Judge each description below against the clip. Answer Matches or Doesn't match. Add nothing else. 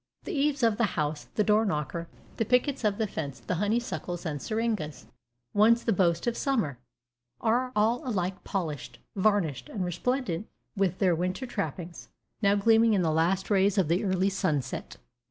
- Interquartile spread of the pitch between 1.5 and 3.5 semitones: Doesn't match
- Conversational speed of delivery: Matches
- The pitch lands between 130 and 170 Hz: Doesn't match